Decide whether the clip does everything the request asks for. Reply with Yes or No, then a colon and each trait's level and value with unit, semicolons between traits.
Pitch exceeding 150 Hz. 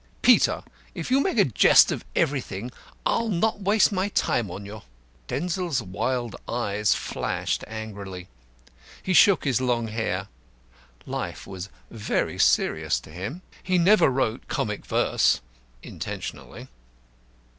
No: low, 125 Hz